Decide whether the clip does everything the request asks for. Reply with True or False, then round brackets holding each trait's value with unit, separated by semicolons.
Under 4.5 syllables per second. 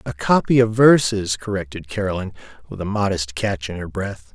False (5.2 syllables/s)